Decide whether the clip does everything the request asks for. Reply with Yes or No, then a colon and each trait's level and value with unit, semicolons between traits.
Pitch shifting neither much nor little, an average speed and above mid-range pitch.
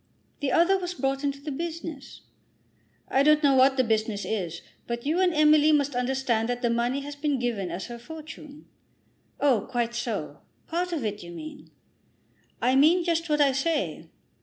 Yes: average, 4.3 semitones; average, 180 wpm; very high, 275 Hz